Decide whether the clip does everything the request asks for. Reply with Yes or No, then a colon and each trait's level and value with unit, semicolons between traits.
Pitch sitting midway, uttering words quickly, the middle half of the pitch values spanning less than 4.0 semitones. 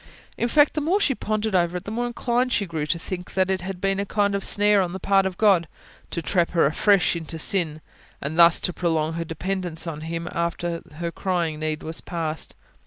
Yes: medium, 180 Hz; fast, 225 wpm; average, 3.2 semitones